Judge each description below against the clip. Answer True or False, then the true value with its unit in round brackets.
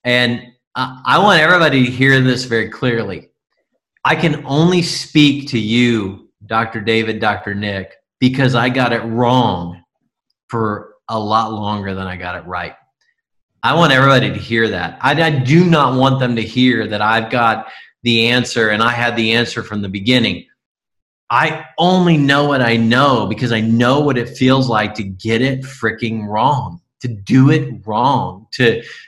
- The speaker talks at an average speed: True (170 wpm)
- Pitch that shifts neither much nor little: True (3.3 semitones)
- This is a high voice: False (120 Hz)